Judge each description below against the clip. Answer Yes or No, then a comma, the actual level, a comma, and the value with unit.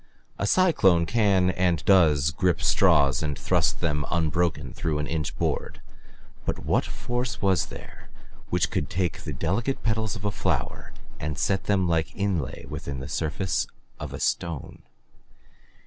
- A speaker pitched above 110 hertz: No, very low, 85 Hz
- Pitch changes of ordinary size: Yes, average, 4.3 semitones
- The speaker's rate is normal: Yes, average, 150 wpm